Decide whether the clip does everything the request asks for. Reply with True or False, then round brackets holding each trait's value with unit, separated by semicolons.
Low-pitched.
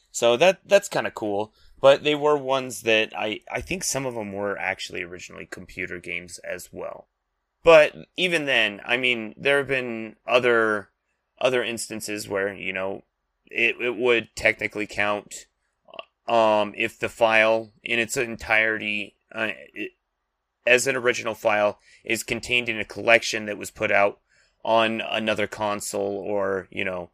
True (110 Hz)